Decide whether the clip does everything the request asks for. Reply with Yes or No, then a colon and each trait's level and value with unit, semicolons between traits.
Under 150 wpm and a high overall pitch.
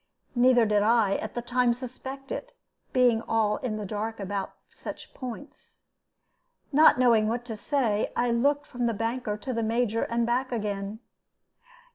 No: average, 160 wpm; high, 235 Hz